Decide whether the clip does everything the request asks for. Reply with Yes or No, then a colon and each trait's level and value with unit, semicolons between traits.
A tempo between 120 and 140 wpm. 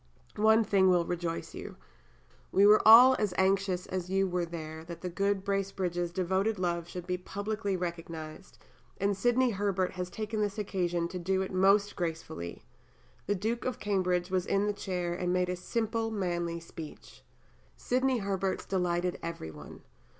No: average, 165 wpm